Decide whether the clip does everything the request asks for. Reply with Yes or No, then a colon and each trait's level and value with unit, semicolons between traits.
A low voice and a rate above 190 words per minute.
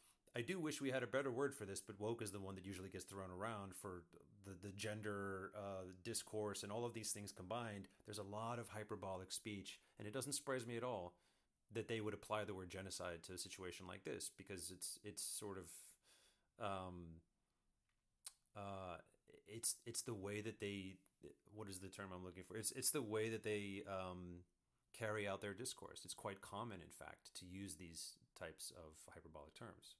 Yes: low, 100 Hz; average, 200 wpm